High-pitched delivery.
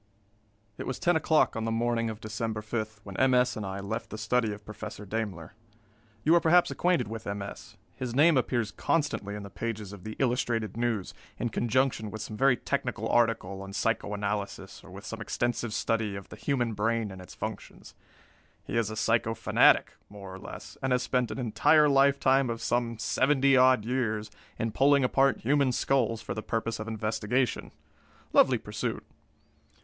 No: low, 115 Hz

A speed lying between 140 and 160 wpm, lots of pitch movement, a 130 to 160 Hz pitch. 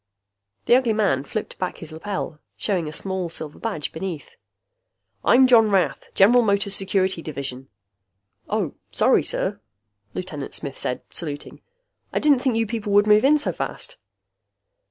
No: average, 150 wpm; wide, 5.8 semitones; high, 195 Hz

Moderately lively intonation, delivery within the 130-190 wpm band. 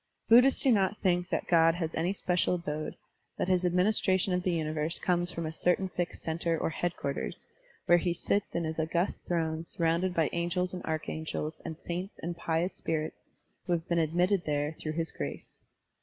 No: narrow, 2.1 semitones; average, 185 wpm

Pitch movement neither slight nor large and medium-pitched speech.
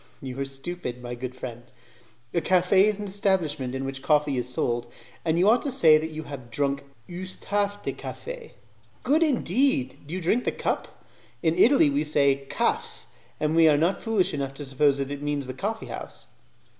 No: wide, 5.9 semitones; medium, 155 Hz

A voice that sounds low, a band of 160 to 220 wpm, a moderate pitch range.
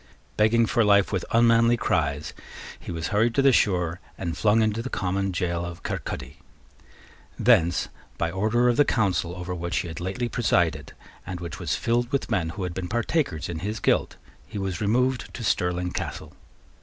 Yes: very low, 95 Hz; average, 180 wpm; average, 5.0 semitones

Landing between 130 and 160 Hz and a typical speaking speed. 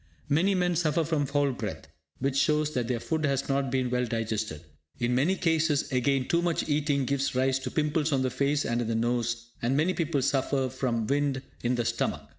No: low, 135 Hz; fast, 210 wpm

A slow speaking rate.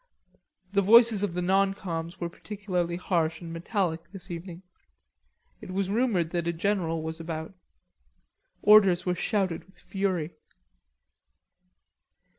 Yes: slow, 125 wpm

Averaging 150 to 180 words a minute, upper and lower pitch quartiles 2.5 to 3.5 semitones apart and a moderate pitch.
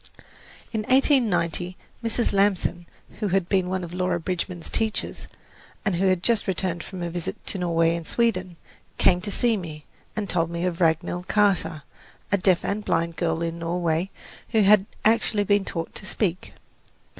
Yes: average, 170 wpm; average, 3.2 semitones; medium, 180 Hz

